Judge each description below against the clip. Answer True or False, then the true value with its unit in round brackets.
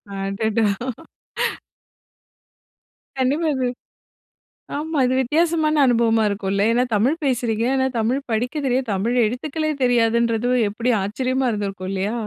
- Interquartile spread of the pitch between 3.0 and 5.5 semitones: True (3.3 semitones)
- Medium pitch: False (240 Hz)